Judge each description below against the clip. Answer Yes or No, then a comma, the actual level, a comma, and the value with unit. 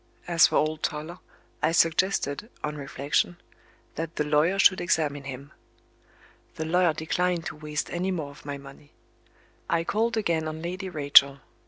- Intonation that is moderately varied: Yes, average, 3.0 semitones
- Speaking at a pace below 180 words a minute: Yes, average, 155 wpm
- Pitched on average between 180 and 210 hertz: No, medium, 160 Hz